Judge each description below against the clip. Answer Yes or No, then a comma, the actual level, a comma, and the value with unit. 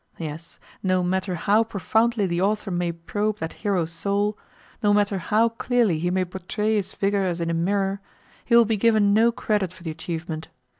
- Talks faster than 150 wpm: Yes, average, 190 wpm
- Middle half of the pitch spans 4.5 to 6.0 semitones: No, average, 3.3 semitones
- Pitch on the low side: No, high, 195 Hz